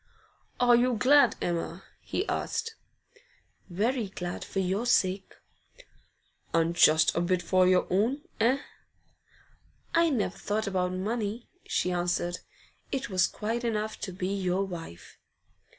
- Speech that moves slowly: Yes, slow, 130 wpm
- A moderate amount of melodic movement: Yes, average, 4.6 semitones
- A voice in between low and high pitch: No, high, 195 Hz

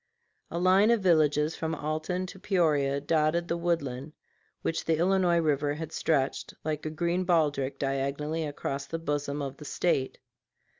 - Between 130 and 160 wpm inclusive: Yes, average, 155 wpm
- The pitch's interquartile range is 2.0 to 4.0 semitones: Yes, average, 2.9 semitones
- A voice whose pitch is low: No, medium, 155 Hz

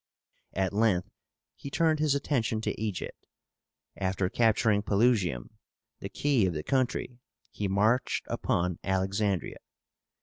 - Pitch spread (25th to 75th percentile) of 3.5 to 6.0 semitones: Yes, average, 4.5 semitones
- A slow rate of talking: Yes, slow, 115 wpm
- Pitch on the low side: Yes, low, 105 Hz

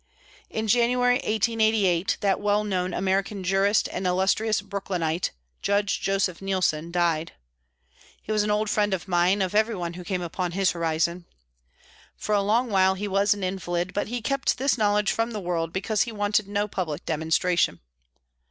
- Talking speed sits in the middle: Yes, average, 165 wpm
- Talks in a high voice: Yes, high, 195 Hz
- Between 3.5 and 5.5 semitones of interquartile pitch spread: No, average, 2.8 semitones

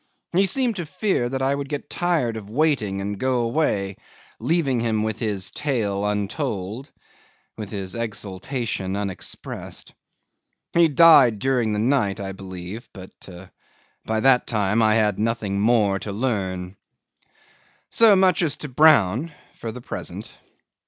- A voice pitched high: No, low, 115 Hz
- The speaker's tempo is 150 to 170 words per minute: No, average, 140 wpm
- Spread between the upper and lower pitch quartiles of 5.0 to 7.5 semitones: Yes, wide, 5.6 semitones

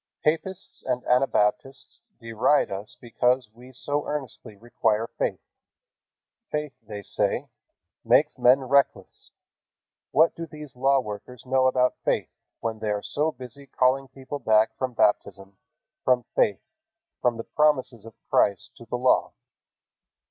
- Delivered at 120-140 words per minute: Yes, slow, 135 wpm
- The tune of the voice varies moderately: Yes, average, 3.3 semitones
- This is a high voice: No, low, 125 Hz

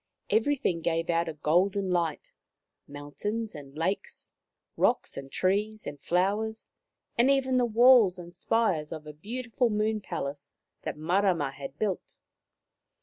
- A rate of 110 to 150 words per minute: Yes, average, 140 wpm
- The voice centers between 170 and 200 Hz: Yes, medium, 185 Hz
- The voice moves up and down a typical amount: No, wide, 6.0 semitones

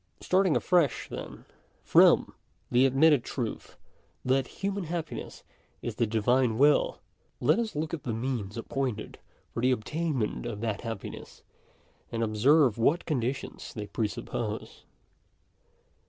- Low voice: Yes, low, 130 Hz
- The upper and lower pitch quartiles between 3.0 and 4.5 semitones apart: No, average, 5.1 semitones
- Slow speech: Yes, slow, 125 wpm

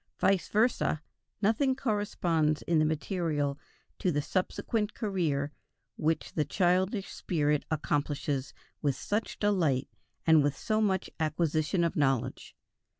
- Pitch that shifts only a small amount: No, average, 5.0 semitones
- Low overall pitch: No, medium, 165 Hz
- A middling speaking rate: No, slow, 120 wpm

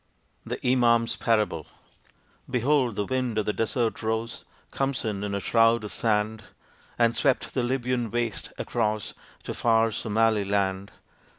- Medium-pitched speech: No, low, 115 Hz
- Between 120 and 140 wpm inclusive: Yes, slow, 135 wpm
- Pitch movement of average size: No, narrow, 2.3 semitones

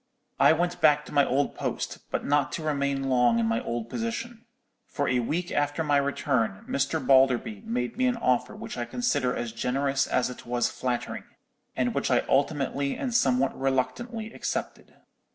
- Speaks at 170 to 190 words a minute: Yes, average, 175 wpm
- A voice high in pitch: No, medium, 140 Hz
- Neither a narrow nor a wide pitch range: Yes, average, 3.6 semitones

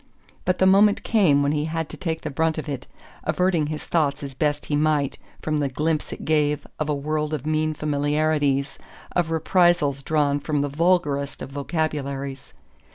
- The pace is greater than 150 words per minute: Yes, average, 180 wpm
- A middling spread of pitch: No, narrow, 2.1 semitones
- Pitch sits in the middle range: Yes, medium, 150 Hz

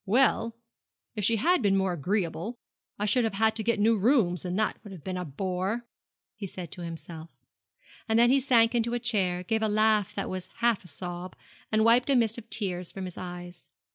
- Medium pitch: No, high, 205 Hz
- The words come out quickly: Yes, fast, 215 wpm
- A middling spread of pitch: Yes, average, 4.0 semitones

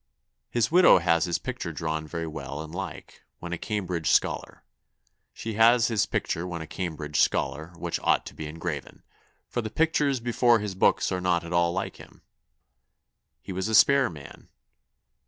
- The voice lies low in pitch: Yes, very low, 90 Hz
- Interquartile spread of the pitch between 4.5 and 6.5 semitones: Yes, wide, 5.4 semitones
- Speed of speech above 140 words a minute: Yes, average, 175 wpm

